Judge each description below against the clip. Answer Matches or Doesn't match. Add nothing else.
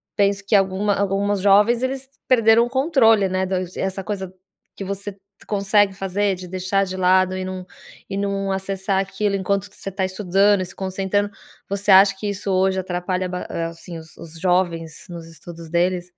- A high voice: Matches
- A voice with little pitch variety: Matches